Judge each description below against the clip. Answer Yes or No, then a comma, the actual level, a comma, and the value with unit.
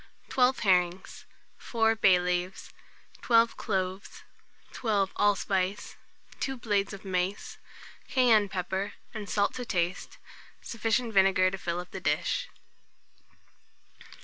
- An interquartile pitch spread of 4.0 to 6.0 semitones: No, average, 3.3 semitones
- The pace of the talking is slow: Yes, slow, 115 wpm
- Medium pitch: No, high, 200 Hz